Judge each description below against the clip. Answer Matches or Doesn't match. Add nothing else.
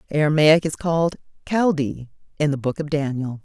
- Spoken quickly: Doesn't match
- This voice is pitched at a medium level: Matches